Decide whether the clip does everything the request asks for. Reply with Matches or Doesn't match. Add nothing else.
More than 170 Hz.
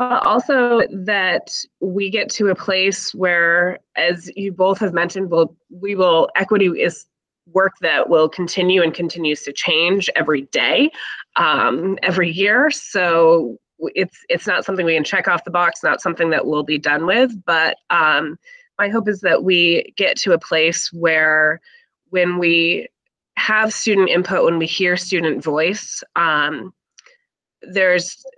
Matches